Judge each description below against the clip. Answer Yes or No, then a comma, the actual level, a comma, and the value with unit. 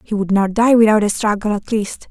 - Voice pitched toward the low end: No, high, 210 Hz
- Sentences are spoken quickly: Yes, fast, 255 wpm